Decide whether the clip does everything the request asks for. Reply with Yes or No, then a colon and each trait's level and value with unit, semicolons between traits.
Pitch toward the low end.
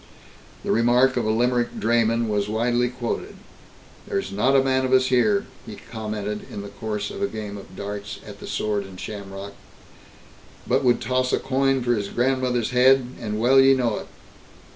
Yes: low, 120 Hz